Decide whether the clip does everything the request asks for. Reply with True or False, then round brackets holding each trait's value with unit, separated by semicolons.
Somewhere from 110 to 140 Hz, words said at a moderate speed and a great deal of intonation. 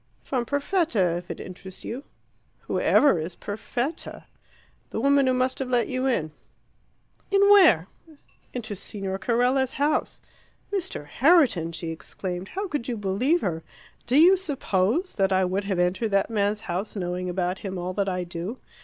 False (210 Hz; 160 wpm; 6.6 semitones)